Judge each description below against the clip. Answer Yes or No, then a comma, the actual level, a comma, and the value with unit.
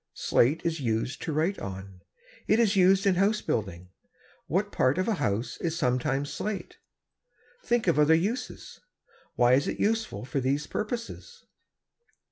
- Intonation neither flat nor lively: No, wide, 8.2 semitones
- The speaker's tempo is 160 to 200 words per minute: No, average, 150 wpm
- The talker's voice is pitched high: No, medium, 160 Hz